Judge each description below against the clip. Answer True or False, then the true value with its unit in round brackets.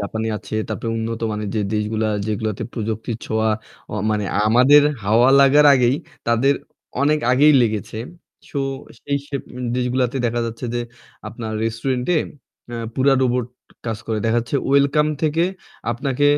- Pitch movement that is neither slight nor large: True (3.7 semitones)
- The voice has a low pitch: True (120 Hz)